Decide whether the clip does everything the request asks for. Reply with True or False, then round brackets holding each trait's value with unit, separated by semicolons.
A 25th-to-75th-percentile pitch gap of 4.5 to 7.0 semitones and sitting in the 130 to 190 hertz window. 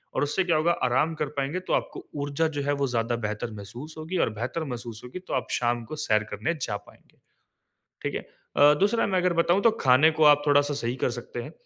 True (4.9 semitones; 140 Hz)